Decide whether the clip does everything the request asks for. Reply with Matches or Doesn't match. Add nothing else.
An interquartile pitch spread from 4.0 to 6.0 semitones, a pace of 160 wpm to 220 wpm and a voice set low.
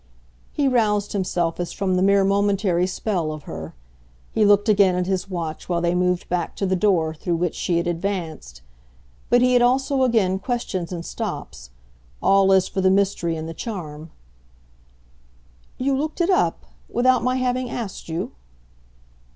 Doesn't match